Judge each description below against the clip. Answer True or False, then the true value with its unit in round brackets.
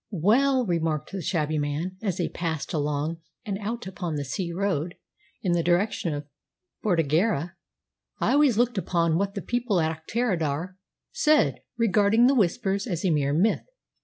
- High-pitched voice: False (180 Hz)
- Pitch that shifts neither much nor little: True (4.9 semitones)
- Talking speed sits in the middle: True (160 wpm)